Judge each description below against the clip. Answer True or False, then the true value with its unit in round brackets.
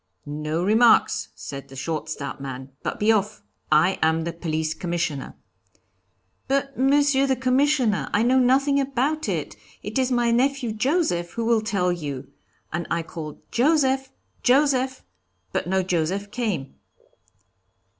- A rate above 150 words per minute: False (140 wpm)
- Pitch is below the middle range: False (215 Hz)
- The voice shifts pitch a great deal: True (8.4 semitones)